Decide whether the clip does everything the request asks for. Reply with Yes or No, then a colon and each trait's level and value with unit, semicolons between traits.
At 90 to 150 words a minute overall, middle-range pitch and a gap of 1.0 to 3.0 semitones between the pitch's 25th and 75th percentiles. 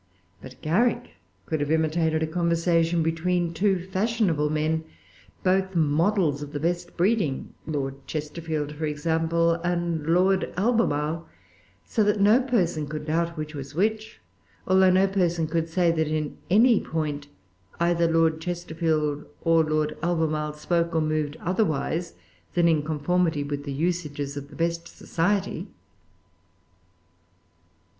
Yes: slow, 135 wpm; medium, 165 Hz; narrow, 2.6 semitones